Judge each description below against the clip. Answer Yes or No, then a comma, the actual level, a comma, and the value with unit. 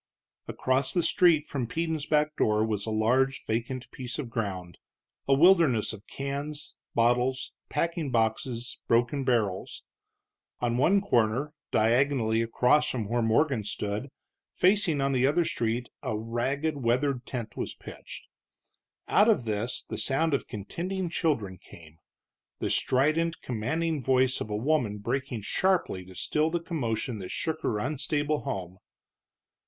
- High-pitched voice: No, low, 130 Hz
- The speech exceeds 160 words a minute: No, average, 140 wpm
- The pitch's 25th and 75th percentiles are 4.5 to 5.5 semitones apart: Yes, average, 5.2 semitones